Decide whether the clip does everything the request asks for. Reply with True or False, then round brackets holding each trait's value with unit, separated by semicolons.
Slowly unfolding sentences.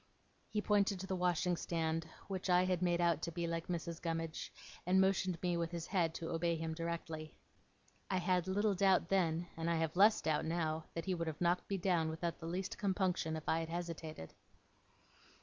False (200 wpm)